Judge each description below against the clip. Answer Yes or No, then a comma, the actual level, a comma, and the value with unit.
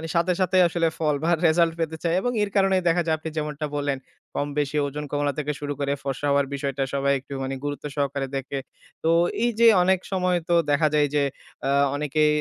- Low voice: No, medium, 150 Hz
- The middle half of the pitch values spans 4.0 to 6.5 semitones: No, average, 2.9 semitones